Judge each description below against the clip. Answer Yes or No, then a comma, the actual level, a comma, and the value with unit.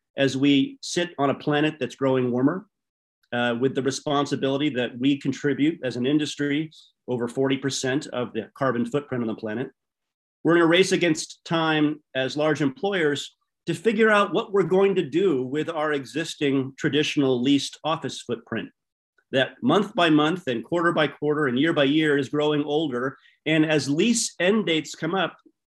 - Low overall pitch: No, medium, 150 Hz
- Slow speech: No, average, 175 wpm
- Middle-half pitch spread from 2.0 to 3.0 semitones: No, average, 3.4 semitones